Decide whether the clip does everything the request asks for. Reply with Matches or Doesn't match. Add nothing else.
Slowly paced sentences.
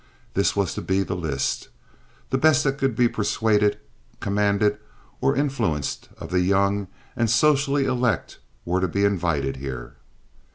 Doesn't match